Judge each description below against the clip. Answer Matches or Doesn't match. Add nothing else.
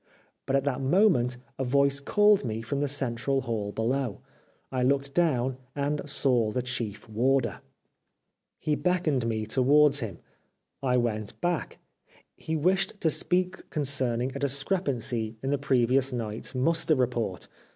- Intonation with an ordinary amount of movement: Matches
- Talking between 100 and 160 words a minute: Matches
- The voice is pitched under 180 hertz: Matches